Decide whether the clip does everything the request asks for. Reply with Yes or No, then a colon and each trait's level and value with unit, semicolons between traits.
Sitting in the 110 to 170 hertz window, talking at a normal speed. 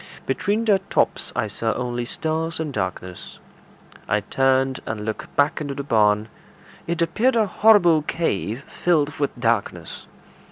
Yes: medium, 140 Hz; average, 145 wpm